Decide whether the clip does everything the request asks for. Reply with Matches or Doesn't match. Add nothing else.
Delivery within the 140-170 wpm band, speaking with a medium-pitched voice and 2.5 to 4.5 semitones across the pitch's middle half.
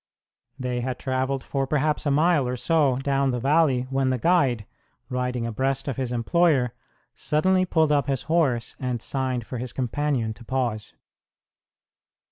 Doesn't match